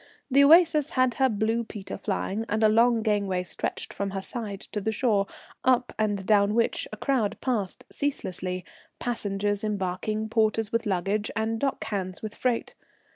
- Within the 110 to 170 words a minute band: Yes, average, 165 wpm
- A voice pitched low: No, high, 215 Hz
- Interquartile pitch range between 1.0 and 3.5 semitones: Yes, average, 2.8 semitones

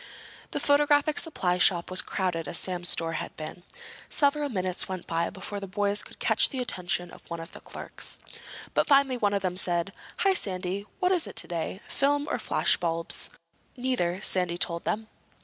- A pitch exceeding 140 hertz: Yes, high, 190 Hz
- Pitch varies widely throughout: Yes, wide, 6.7 semitones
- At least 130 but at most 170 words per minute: No, average, 185 wpm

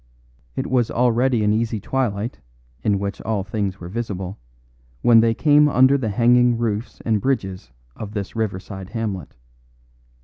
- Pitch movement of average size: Yes, average, 3.3 semitones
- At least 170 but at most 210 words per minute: No, average, 145 wpm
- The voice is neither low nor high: No, low, 110 Hz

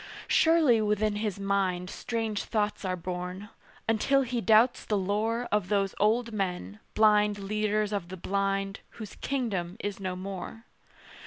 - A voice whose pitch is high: Yes, high, 205 Hz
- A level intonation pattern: Yes, narrow, 2.3 semitones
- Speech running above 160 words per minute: No, average, 145 wpm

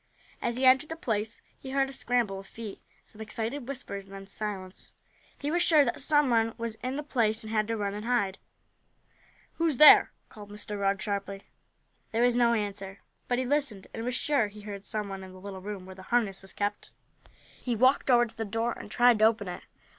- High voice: Yes, high, 220 Hz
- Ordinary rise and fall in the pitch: Yes, average, 3.6 semitones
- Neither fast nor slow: No, fast, 215 wpm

